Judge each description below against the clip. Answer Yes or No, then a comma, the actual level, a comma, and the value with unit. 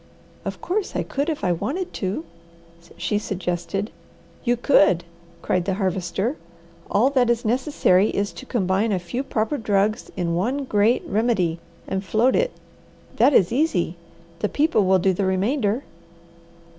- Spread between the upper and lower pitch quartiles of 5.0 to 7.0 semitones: Yes, average, 5.3 semitones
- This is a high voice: Yes, high, 210 Hz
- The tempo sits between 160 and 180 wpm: No, average, 150 wpm